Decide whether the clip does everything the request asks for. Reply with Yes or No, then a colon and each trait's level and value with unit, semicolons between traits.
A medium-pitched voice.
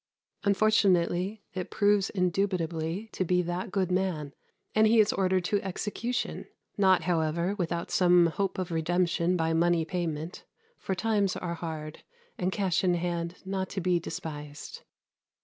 Yes: medium, 180 Hz